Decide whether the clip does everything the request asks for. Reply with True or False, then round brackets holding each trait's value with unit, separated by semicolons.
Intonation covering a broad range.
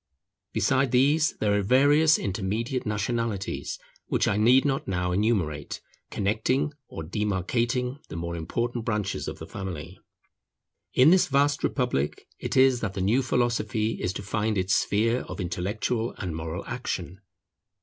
False (4.8 semitones)